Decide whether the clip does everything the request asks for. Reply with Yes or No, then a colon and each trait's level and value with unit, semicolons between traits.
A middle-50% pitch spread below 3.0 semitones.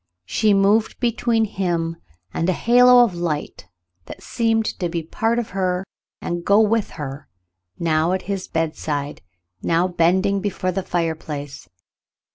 No: average, 4.4 semitones